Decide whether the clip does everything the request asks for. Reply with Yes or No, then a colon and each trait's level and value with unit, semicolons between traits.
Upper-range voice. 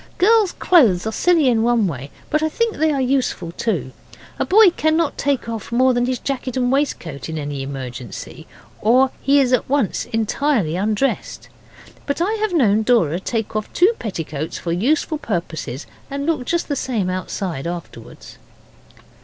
Yes: high, 240 Hz